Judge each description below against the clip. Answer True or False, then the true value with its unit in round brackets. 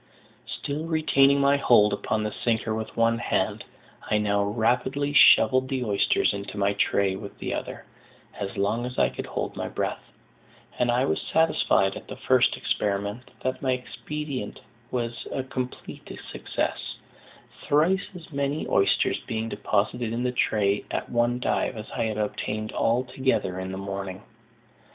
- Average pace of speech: True (155 wpm)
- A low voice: True (115 Hz)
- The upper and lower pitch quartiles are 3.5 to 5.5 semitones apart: True (4.2 semitones)